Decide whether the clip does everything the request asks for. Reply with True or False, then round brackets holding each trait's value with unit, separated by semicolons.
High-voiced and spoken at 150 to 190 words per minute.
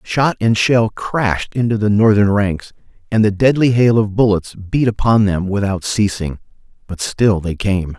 False (105 Hz; 175 wpm)